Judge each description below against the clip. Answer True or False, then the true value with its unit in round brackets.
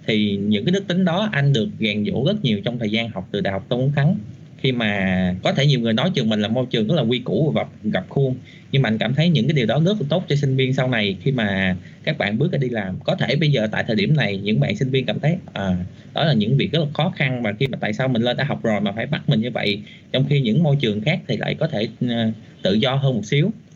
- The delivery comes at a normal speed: False (305 wpm)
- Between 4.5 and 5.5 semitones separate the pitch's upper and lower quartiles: True (5.2 semitones)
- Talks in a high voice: False (130 Hz)